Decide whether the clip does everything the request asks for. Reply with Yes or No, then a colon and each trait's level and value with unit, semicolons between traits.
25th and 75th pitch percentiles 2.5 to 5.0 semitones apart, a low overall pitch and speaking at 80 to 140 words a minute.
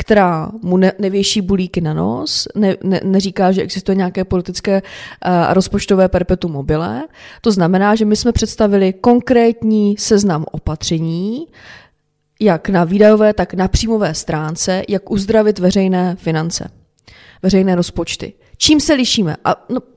No: average, 2.8 semitones; high, 195 Hz; average, 135 wpm